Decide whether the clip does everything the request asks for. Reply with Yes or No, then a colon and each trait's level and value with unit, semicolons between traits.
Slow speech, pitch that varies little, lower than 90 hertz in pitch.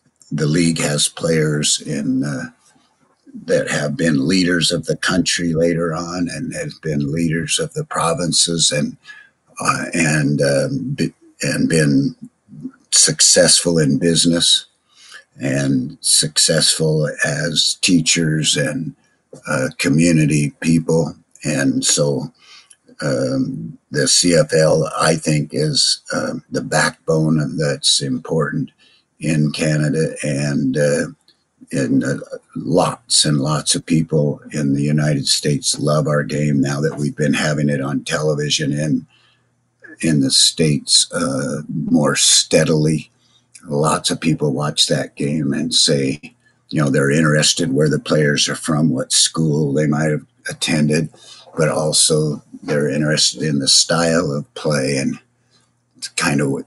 Yes: slow, 130 wpm; narrow, 2.0 semitones; very low, 75 Hz